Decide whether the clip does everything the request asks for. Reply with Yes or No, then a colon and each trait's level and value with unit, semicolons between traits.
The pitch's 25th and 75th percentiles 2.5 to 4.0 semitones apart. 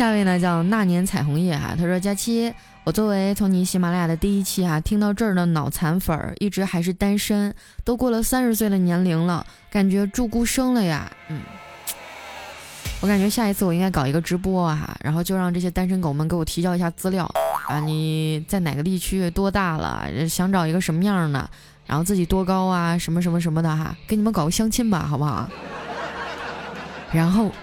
Yes: average, 3.4 semitones